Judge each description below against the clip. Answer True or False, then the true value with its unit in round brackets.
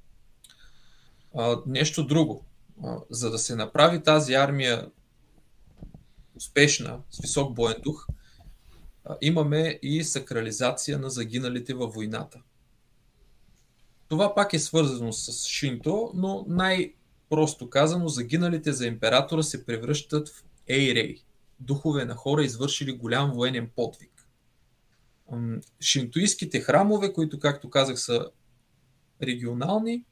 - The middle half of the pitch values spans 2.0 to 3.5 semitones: False (4.1 semitones)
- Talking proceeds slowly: True (100 wpm)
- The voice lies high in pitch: False (140 Hz)